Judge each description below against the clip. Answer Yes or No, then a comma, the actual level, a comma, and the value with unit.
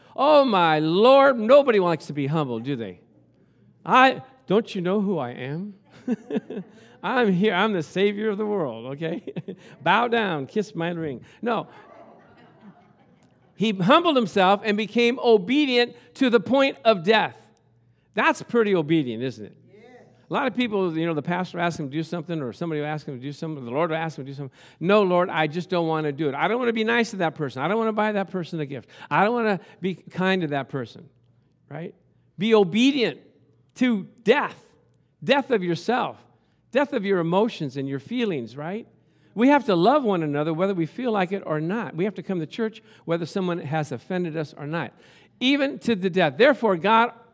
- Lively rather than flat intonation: Yes, wide, 6.3 semitones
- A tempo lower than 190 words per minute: No, fast, 205 wpm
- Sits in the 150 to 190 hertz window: Yes, medium, 185 Hz